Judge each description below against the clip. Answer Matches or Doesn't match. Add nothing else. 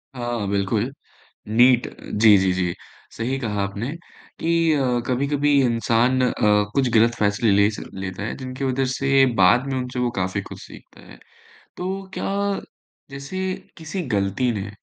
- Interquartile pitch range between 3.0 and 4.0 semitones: Doesn't match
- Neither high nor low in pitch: Doesn't match